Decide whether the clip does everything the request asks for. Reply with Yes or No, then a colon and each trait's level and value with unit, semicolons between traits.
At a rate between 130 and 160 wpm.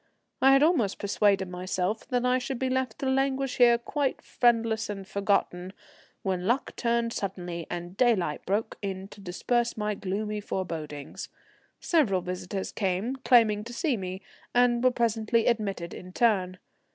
Yes: average, 155 wpm